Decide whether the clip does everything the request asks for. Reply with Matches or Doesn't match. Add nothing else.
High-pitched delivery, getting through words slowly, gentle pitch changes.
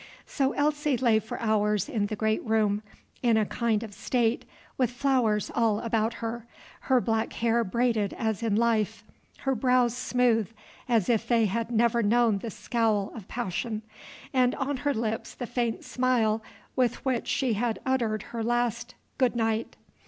Doesn't match